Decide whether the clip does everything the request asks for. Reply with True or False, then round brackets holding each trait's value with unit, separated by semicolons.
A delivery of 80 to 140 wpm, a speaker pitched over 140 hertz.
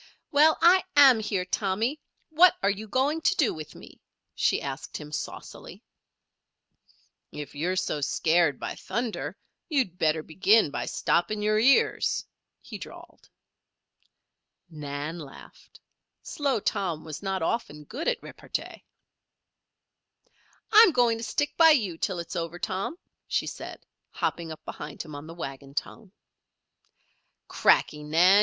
True (135 wpm; 190 Hz)